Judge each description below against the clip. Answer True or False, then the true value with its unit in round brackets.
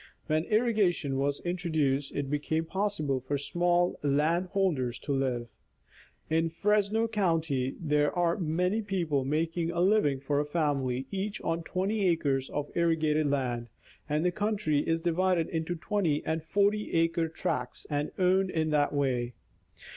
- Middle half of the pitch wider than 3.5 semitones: True (4.0 semitones)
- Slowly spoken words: False (145 wpm)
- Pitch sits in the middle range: True (160 Hz)